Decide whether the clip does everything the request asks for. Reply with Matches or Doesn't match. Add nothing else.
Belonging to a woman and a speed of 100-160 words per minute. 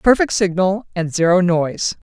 Matches